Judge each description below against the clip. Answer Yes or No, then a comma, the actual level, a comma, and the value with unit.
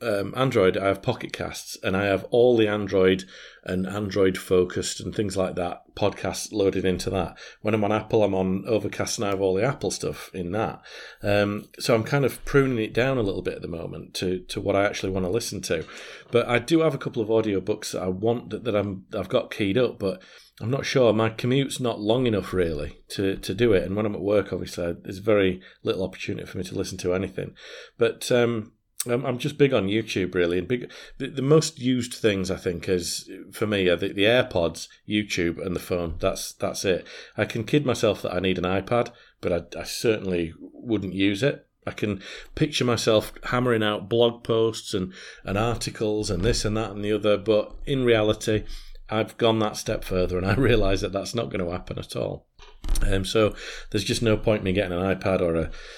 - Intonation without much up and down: No, average, 3.5 semitones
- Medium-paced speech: No, fast, 220 wpm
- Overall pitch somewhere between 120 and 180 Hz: No, low, 105 Hz